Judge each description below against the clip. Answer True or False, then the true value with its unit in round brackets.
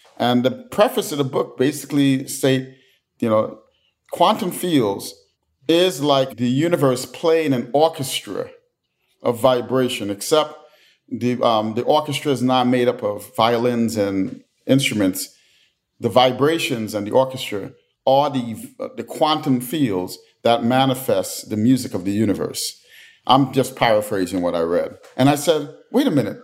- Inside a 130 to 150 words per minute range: True (145 wpm)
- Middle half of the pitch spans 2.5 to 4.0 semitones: True (3.5 semitones)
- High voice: False (130 Hz)